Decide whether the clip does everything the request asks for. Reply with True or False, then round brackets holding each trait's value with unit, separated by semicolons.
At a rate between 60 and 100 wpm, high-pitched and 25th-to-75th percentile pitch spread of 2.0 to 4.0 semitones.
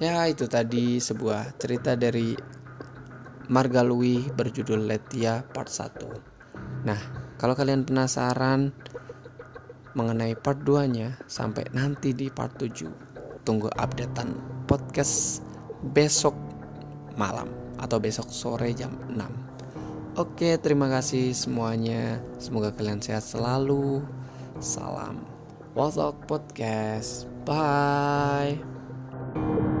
False (95 wpm; 130 Hz; 2.9 semitones)